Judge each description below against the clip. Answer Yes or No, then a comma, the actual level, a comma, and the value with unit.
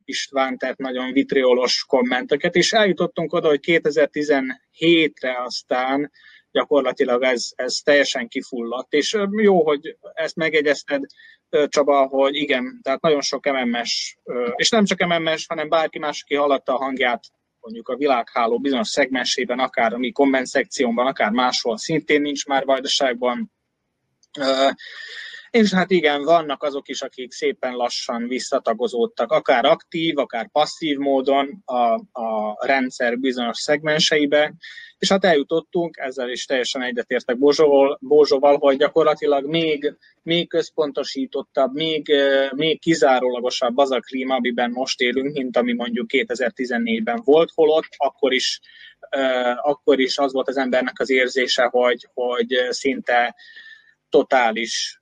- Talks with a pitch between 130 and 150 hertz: Yes, medium, 140 Hz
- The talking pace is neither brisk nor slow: Yes, average, 130 wpm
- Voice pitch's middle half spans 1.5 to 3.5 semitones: No, average, 4.2 semitones